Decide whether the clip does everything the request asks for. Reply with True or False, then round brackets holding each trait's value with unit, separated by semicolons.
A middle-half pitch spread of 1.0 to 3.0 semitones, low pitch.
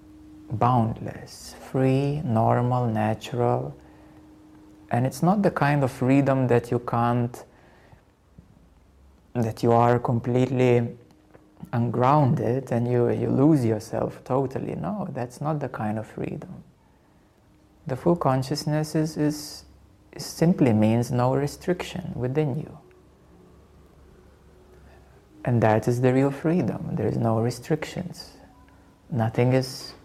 False (4.6 semitones; 120 Hz)